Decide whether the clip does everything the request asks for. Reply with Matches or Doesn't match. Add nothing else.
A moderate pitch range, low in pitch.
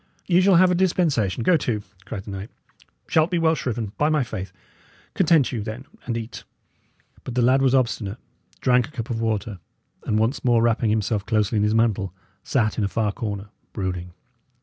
Matches